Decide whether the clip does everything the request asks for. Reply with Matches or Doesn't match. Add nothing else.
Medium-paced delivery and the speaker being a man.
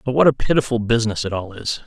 Doesn't match